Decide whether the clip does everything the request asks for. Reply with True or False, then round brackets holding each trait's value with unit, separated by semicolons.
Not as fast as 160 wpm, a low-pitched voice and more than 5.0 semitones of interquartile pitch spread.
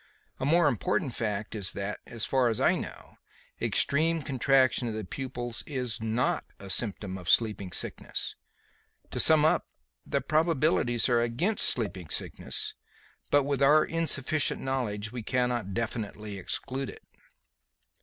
False (140 wpm; 120 Hz; 4.7 semitones)